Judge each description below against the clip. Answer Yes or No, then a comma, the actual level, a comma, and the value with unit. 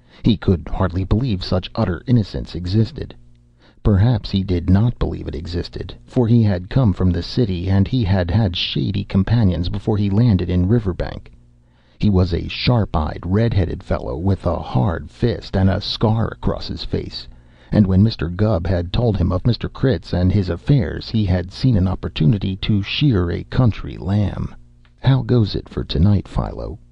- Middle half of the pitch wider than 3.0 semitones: Yes, average, 4.0 semitones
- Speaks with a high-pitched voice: No, very low, 95 Hz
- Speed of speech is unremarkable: Yes, average, 175 wpm